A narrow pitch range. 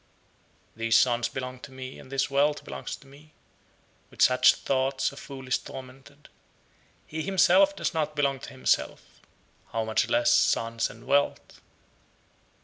Yes: narrow, 2.2 semitones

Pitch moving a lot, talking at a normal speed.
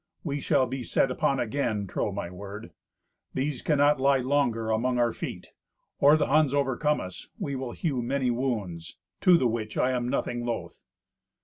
No: average, 3.6 semitones; average, 175 wpm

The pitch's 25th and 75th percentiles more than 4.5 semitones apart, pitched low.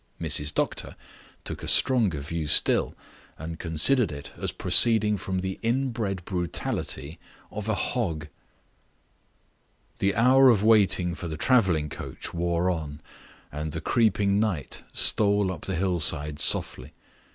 Yes: average, 5.2 semitones; very low, 95 Hz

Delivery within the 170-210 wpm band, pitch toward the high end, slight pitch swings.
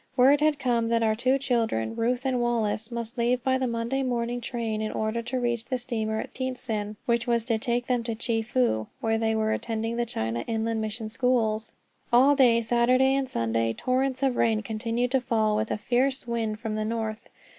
Yes: average, 200 wpm; high, 235 Hz; narrow, 2.2 semitones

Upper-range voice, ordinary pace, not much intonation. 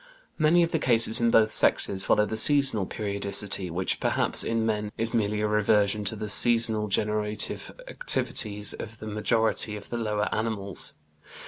No: low, 105 Hz; average, 160 wpm; narrow, 1.7 semitones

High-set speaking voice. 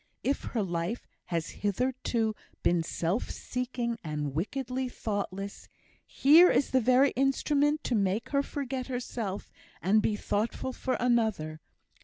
Yes: high, 235 Hz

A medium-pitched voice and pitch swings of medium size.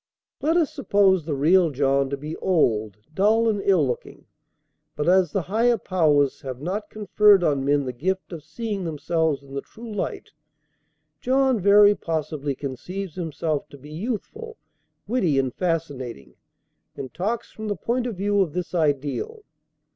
No: medium, 175 Hz; wide, 6.3 semitones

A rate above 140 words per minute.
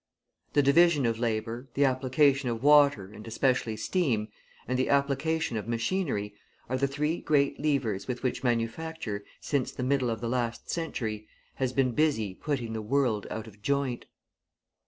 Yes: average, 160 wpm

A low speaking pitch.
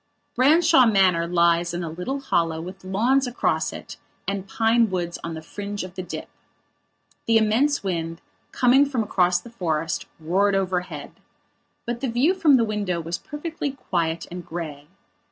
No: high, 190 Hz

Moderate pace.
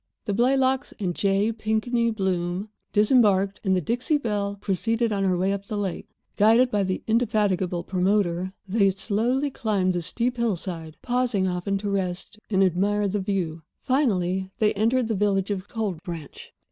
Yes: average, 160 wpm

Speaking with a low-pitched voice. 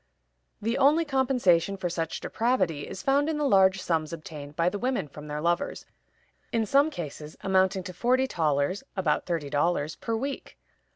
No: medium, 185 Hz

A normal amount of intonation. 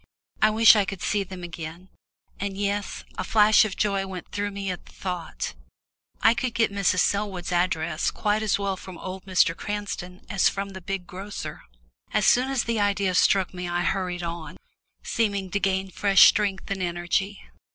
No: narrow, 2.2 semitones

